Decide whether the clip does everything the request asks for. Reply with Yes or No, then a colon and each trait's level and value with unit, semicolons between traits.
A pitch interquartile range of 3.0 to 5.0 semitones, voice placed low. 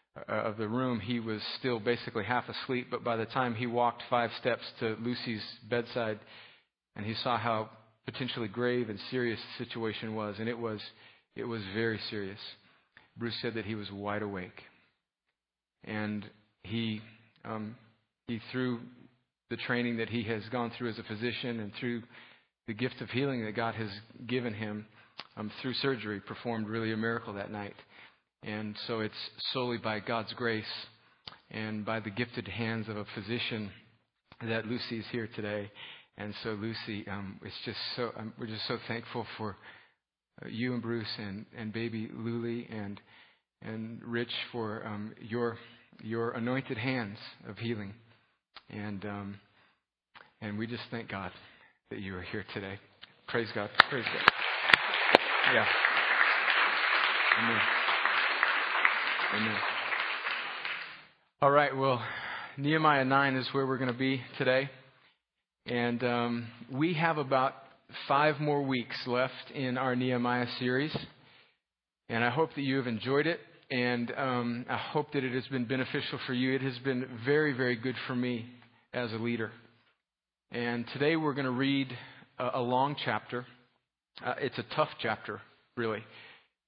No: narrow, 2.4 semitones; low, 120 Hz